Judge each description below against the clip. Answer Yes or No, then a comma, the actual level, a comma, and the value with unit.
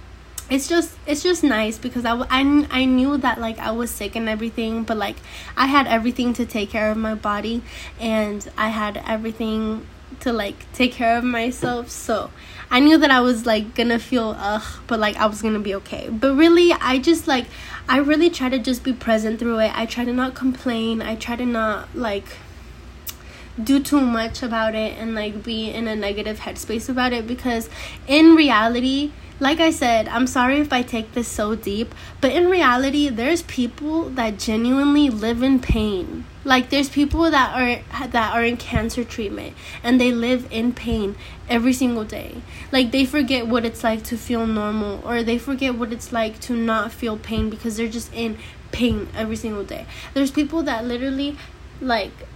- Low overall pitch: No, high, 240 Hz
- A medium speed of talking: Yes, average, 190 wpm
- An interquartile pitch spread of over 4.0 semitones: No, average, 2.9 semitones